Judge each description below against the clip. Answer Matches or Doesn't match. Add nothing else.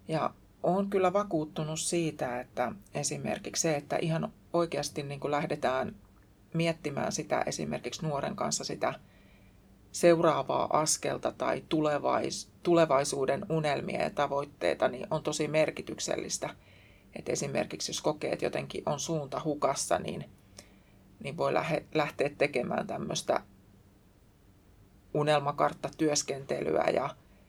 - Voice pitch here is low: Doesn't match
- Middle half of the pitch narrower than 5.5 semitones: Doesn't match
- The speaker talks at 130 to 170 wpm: Doesn't match